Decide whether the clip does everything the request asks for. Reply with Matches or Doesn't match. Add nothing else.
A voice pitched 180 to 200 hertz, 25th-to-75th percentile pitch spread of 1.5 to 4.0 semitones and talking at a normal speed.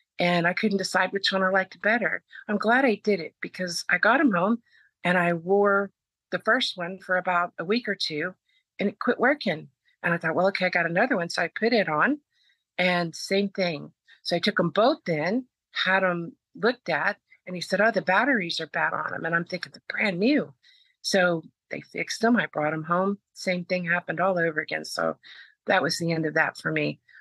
Doesn't match